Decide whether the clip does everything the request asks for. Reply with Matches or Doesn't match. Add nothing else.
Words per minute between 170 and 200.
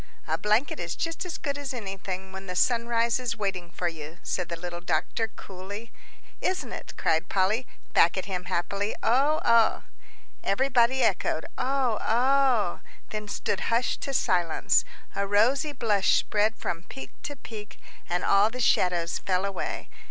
Doesn't match